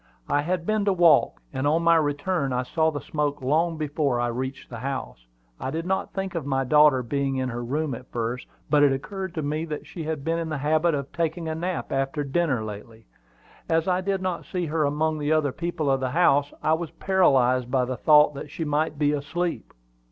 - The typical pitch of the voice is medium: Yes, medium, 150 Hz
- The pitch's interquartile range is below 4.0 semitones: Yes, average, 3.6 semitones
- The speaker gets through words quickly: Yes, fast, 225 wpm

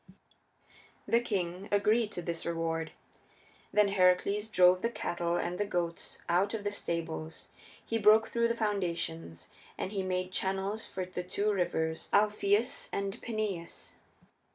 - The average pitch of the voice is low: No, high, 190 Hz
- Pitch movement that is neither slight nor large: Yes, average, 3.3 semitones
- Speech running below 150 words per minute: Yes, average, 140 wpm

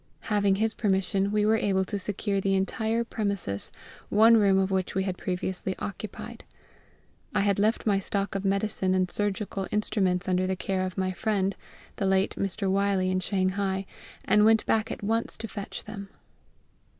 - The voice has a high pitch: Yes, high, 195 Hz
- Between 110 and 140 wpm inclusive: No, average, 175 wpm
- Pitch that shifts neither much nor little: No, narrow, 1.7 semitones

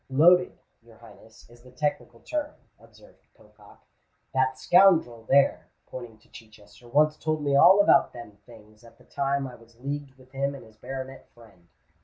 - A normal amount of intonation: Yes, average, 3.8 semitones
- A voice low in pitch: Yes, low, 130 Hz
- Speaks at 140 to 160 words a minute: No, average, 170 wpm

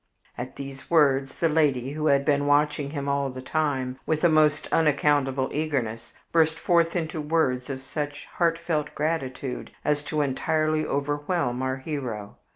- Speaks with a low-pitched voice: No, medium, 145 Hz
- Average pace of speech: Yes, average, 155 wpm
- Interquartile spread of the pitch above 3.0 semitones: No, average, 2.7 semitones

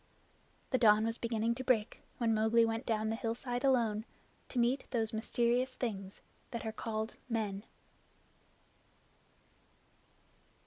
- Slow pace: Yes, slow, 125 wpm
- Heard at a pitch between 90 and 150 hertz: No, high, 230 Hz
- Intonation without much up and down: Yes, narrow, 1.8 semitones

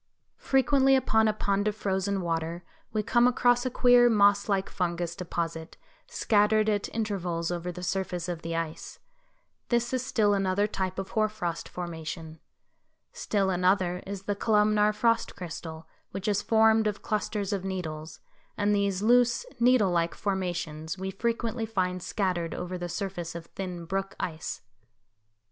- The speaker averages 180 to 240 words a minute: No, average, 155 wpm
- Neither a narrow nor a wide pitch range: Yes, average, 3.5 semitones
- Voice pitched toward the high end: Yes, high, 195 Hz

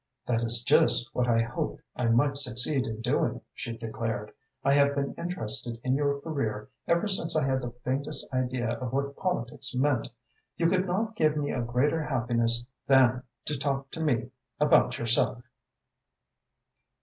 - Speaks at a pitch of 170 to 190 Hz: No, low, 130 Hz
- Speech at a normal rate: Yes, average, 160 wpm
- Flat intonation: No, average, 3.4 semitones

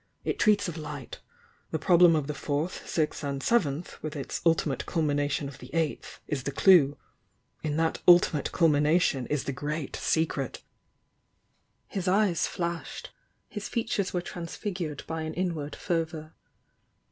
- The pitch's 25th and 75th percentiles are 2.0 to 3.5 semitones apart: Yes, average, 3.2 semitones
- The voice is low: No, medium, 160 Hz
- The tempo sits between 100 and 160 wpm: Yes, average, 155 wpm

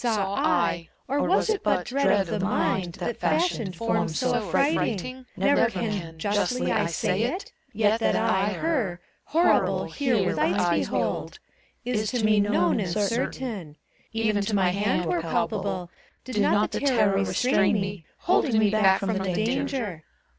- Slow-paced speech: No, average, 160 wpm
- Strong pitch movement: No, average, 4.2 semitones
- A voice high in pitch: Yes, high, 210 Hz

